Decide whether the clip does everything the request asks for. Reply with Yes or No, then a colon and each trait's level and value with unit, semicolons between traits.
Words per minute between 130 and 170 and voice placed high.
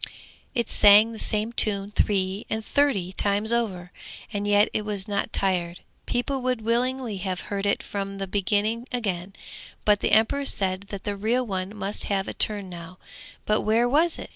No: average, 185 wpm; high, 205 Hz